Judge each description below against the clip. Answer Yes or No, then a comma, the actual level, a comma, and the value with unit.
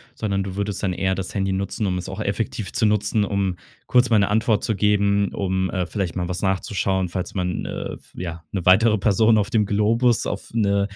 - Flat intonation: Yes, narrow, 2.0 semitones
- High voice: No, low, 100 Hz